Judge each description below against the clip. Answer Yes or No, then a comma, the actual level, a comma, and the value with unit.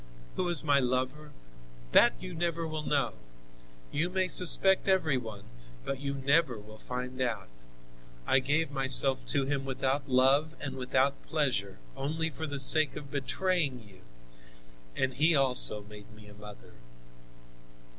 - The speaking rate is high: No, average, 145 wpm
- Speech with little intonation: No, average, 3.6 semitones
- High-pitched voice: No, low, 135 Hz